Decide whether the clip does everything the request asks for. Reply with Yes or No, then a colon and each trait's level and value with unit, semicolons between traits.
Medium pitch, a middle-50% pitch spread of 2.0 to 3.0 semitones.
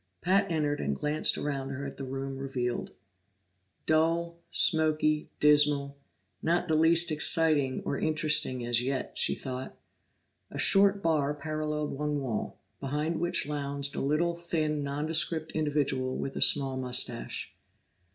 Yes: medium, 150 Hz; narrow, 2.6 semitones